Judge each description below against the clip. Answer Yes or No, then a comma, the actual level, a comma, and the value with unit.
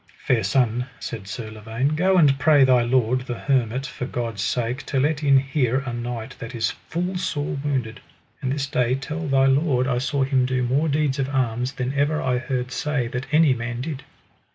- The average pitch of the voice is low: Yes, low, 130 Hz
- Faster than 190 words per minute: Yes, average, 200 wpm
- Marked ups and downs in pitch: No, narrow, 2.6 semitones